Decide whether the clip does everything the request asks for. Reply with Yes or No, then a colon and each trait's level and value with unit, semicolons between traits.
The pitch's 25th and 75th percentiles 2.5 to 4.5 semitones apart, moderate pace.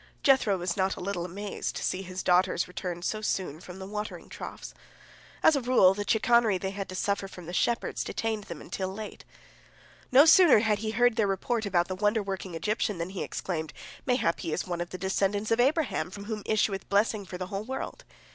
No: average, 3.0 semitones; fast, 215 wpm